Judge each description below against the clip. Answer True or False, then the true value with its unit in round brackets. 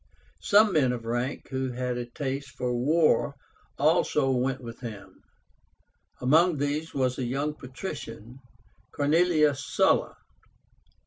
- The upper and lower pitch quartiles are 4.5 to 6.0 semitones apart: False (3.5 semitones)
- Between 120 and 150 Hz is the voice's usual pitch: True (135 Hz)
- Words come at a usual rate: False (120 wpm)